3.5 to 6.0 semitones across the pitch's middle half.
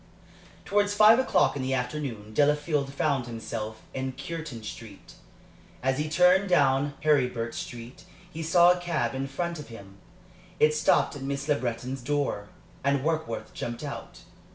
Yes: average, 4.2 semitones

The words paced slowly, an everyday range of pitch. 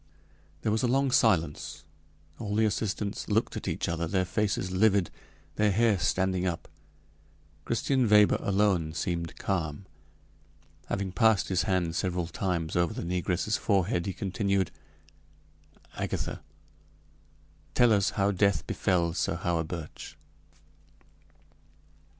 Yes: slow, 120 wpm; average, 3.2 semitones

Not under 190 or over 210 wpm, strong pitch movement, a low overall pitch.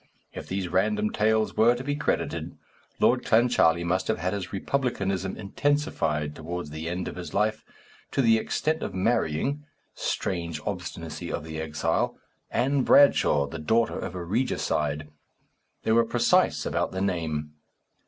No: average, 150 wpm; wide, 6.0 semitones; very low, 95 Hz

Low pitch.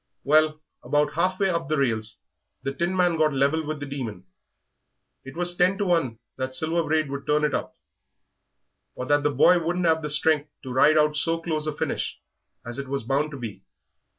No: medium, 150 Hz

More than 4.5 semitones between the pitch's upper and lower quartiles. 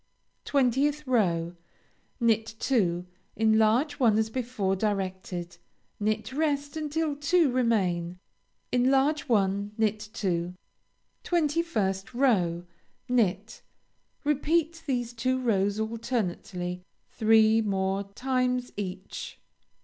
Yes: average, 5.3 semitones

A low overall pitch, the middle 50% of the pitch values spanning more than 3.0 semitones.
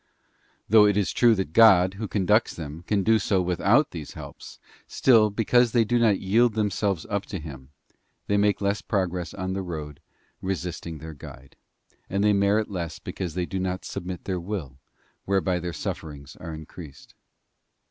Yes: very low, 95 Hz; average, 3.7 semitones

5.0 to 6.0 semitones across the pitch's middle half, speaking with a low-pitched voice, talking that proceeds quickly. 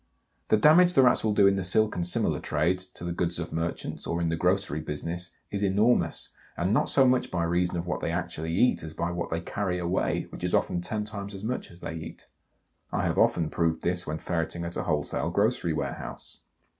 No: average, 3.3 semitones; very low, 90 Hz; fast, 225 wpm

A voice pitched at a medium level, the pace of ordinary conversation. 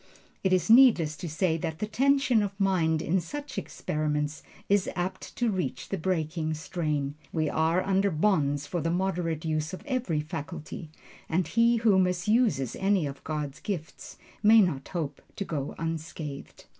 Yes: medium, 170 Hz; average, 160 wpm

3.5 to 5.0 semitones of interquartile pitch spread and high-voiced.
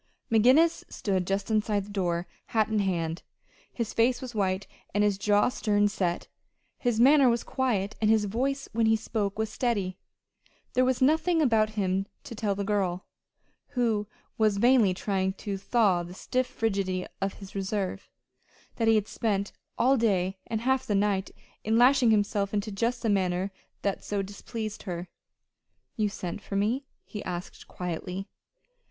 No: average, 3.1 semitones; high, 210 Hz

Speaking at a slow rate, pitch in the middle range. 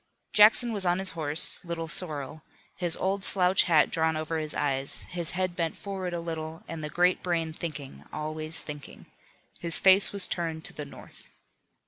No: average, 180 wpm; medium, 165 Hz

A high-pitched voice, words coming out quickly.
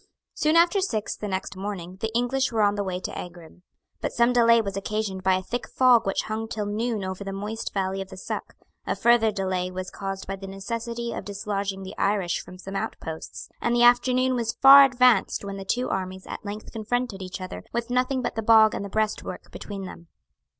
Yes: high, 210 Hz; fast, 215 wpm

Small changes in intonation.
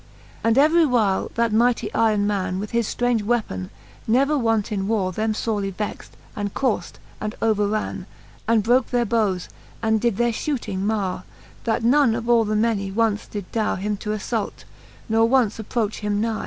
Yes: narrow, 2.2 semitones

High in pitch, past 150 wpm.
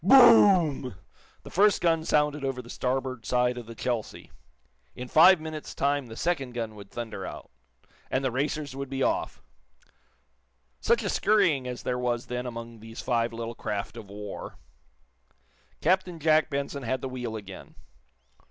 No: low, 130 Hz; average, 160 wpm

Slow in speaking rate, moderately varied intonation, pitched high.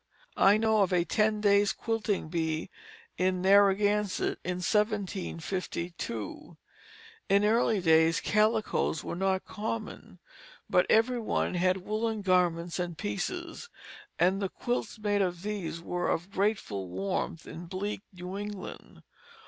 Yes: slow, 125 wpm; average, 3.1 semitones; high, 195 Hz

